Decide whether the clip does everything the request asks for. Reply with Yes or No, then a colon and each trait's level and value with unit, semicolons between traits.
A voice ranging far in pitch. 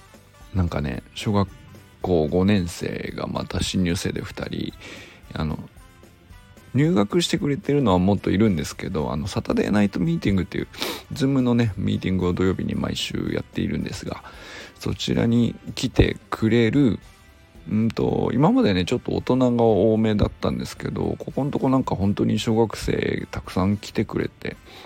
No: average, 4.0 semitones